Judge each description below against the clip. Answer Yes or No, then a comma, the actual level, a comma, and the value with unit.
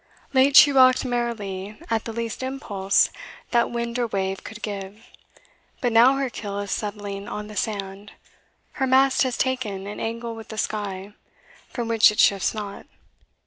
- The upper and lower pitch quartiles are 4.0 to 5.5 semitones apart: No, average, 3.2 semitones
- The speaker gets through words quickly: No, average, 165 wpm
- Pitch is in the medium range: No, high, 220 Hz